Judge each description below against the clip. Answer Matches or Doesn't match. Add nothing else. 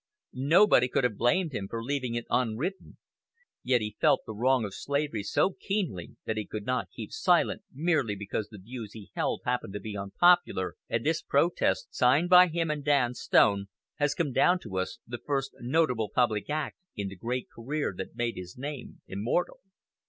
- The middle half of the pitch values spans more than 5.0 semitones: Matches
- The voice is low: Matches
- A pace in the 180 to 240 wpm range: Matches